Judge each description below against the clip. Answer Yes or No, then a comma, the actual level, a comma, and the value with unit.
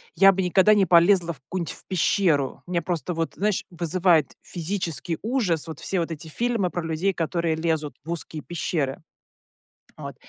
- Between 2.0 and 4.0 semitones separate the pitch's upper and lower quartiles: Yes, average, 2.7 semitones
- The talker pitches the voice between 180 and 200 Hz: No, medium, 170 Hz